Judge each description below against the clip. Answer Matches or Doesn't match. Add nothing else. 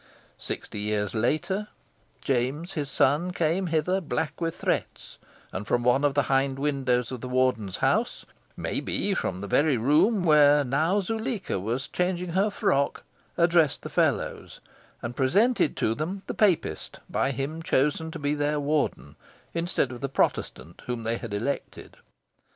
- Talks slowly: Doesn't match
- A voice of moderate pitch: Matches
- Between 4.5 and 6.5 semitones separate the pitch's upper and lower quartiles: Matches